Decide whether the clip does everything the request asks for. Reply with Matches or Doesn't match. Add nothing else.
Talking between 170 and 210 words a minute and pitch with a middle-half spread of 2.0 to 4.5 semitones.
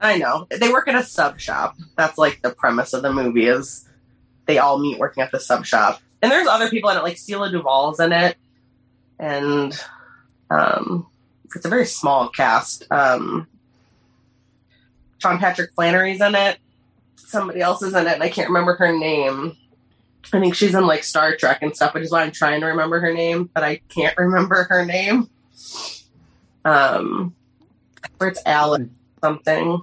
Doesn't match